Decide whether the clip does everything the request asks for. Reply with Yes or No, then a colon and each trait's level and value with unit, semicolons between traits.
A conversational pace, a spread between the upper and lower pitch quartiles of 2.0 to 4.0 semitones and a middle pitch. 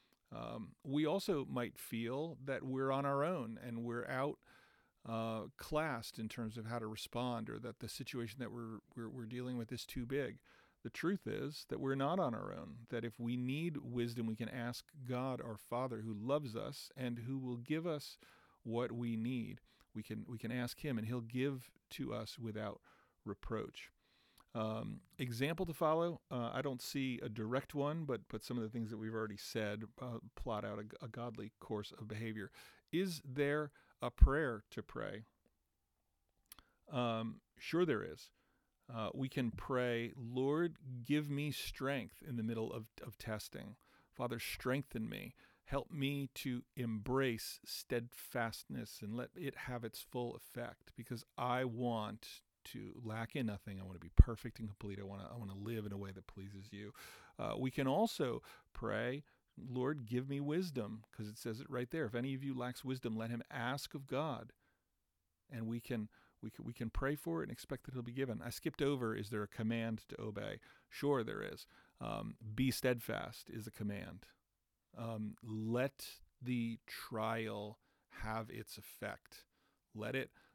No: average, 180 wpm; average, 3.1 semitones; low, 120 Hz